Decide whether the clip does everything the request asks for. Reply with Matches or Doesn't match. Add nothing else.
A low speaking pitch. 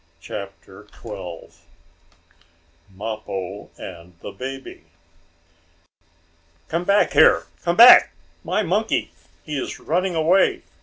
Matches